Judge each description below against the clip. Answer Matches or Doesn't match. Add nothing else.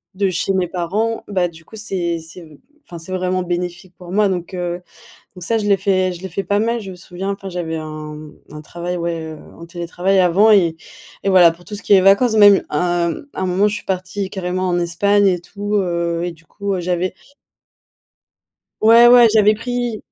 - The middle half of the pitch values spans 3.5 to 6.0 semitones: Doesn't match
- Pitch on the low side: Doesn't match